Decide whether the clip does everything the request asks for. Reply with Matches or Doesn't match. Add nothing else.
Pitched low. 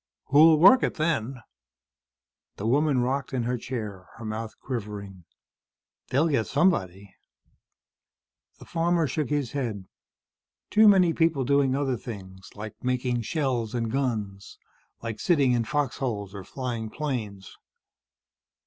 Matches